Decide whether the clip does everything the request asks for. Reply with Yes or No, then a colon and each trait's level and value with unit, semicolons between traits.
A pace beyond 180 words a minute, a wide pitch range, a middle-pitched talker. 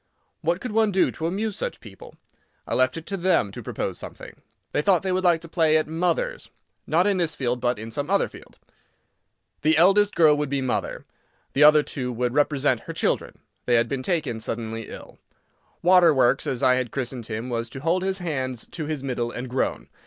Yes: fast, 205 wpm; wide, 5.7 semitones; medium, 150 Hz